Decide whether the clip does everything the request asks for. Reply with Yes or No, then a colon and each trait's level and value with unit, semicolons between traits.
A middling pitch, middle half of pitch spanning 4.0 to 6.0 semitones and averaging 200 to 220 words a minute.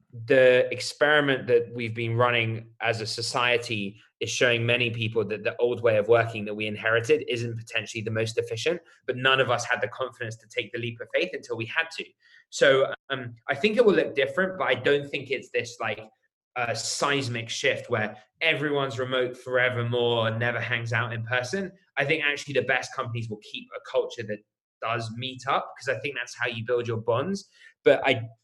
No: low, 125 Hz; average, 4.3 semitones; fast, 205 wpm